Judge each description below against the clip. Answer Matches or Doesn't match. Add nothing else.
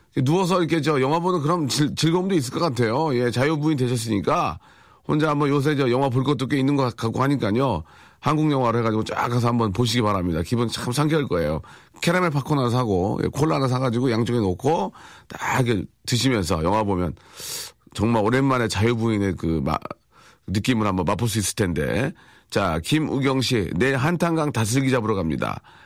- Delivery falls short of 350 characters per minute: Doesn't match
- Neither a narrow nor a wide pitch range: Matches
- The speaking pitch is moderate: Doesn't match